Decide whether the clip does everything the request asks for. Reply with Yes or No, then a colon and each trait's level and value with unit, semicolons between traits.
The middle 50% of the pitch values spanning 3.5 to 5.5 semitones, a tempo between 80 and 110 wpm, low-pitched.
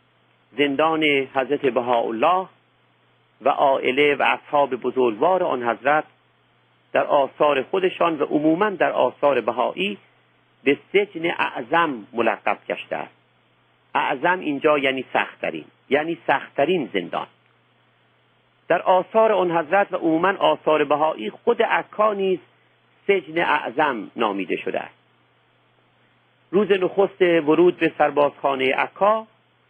No: average, 5.1 semitones; slow, 105 wpm; medium, 155 Hz